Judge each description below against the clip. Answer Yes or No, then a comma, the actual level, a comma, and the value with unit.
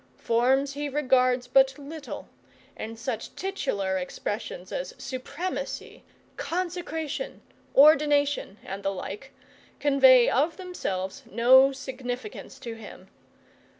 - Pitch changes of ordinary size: Yes, average, 4.1 semitones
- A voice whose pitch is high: Yes, very high, 265 Hz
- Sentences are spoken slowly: Yes, slow, 100 wpm